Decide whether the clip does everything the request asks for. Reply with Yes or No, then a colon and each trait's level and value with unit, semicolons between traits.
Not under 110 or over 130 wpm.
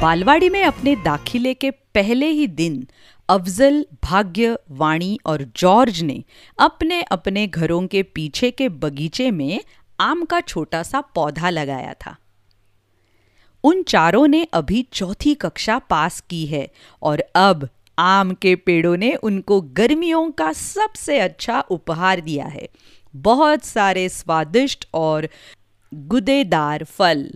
Yes: average, 125 wpm